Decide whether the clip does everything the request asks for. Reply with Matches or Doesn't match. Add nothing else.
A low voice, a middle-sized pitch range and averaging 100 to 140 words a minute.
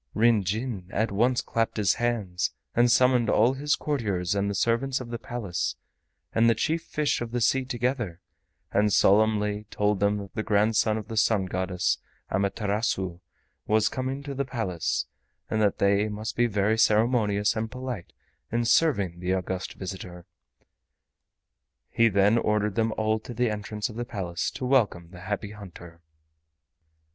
Doesn't match